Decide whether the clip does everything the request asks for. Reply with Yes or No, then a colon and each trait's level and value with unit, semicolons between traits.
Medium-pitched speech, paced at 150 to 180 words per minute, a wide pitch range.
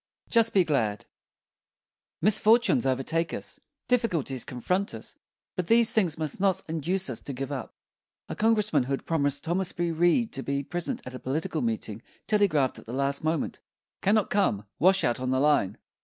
Yes: medium, 160 Hz; average, 170 wpm; wide, 6.4 semitones